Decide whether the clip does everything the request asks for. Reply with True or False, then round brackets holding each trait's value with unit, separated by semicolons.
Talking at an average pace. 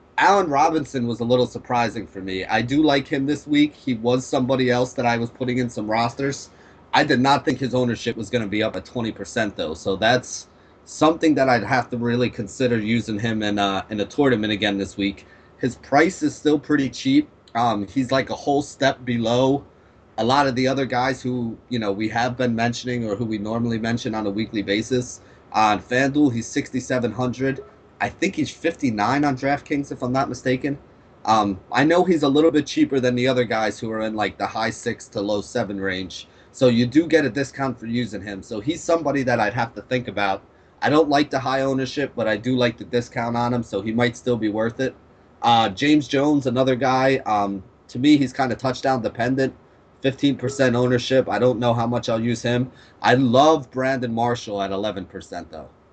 False (215 wpm)